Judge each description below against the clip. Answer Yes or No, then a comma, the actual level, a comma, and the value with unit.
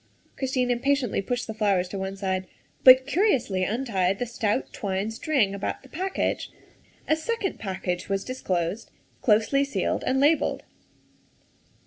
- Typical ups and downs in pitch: No, wide, 5.7 semitones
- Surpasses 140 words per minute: No, slow, 135 wpm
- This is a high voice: Yes, high, 225 Hz